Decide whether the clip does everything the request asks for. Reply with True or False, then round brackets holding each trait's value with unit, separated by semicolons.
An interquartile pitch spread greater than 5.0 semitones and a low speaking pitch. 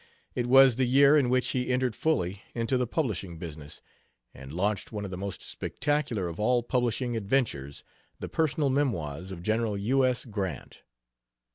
True (5.4 semitones; 115 Hz)